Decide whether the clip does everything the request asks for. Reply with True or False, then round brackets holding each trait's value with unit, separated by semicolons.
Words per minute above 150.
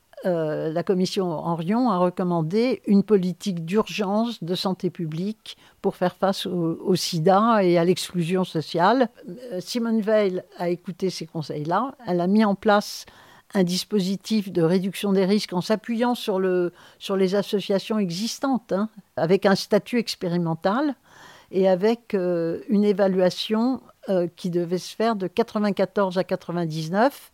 False (145 wpm)